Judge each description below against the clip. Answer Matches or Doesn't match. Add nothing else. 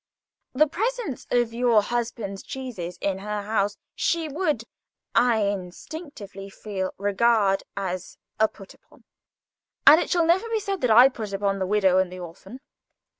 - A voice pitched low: Doesn't match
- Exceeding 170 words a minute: Doesn't match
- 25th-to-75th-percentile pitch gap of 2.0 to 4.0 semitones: Doesn't match